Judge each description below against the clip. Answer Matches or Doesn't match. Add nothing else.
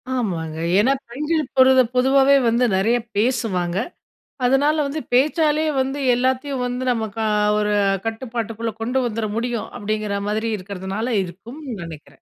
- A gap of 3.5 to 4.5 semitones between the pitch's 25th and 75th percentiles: Matches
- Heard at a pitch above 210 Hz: Matches